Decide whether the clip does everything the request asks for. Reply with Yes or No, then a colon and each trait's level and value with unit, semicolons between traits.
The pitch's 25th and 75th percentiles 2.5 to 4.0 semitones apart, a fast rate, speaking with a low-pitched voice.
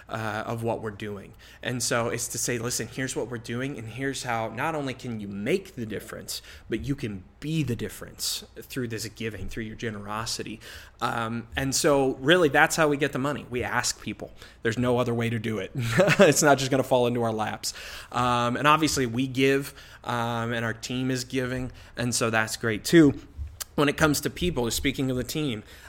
Yes: average, 3.4 semitones; fast, 210 wpm; low, 120 Hz